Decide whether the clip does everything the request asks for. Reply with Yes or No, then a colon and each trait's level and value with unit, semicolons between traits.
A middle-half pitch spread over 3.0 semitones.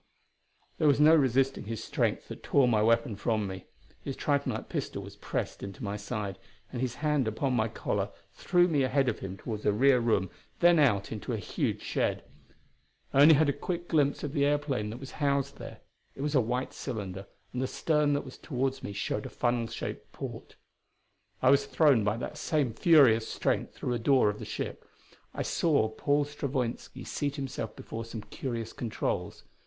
Yes: average, 4.5 semitones